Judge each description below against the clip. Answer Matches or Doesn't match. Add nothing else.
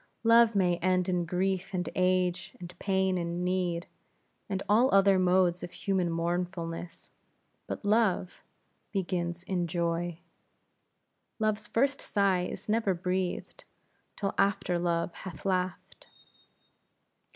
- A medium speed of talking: Doesn't match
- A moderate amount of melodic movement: Doesn't match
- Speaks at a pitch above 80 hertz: Matches